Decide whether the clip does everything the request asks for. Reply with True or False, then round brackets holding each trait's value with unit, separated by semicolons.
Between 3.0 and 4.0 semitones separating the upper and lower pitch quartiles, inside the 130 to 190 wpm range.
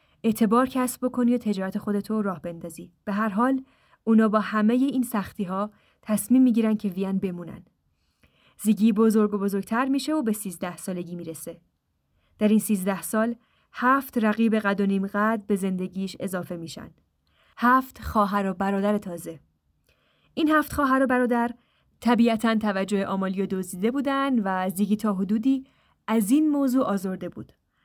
True (3.7 semitones; 150 wpm)